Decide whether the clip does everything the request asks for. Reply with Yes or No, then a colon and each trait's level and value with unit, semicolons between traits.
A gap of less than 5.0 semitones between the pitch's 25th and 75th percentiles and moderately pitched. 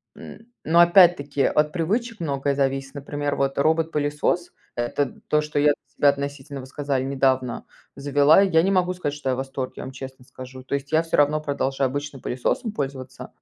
Yes: average, 2.7 semitones; medium, 145 Hz